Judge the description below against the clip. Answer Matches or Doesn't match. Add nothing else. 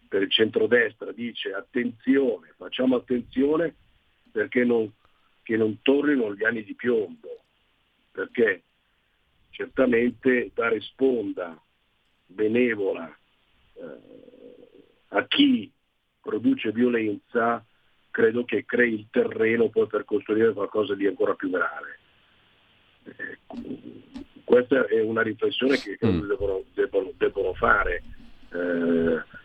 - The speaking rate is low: Matches